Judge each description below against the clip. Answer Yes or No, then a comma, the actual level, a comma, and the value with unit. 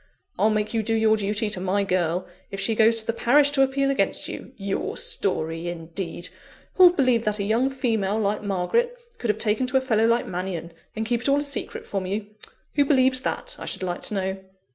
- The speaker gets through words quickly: Yes, fast, 220 wpm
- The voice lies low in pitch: No, high, 215 Hz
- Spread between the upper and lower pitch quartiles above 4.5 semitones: Yes, average, 4.9 semitones